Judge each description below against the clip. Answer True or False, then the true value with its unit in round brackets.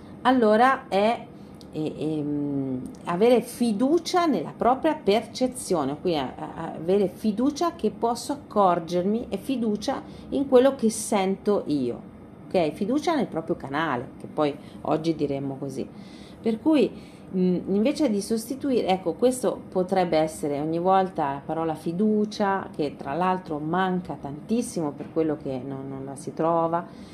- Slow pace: False (130 wpm)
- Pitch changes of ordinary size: False (6.8 semitones)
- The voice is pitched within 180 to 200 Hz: True (190 Hz)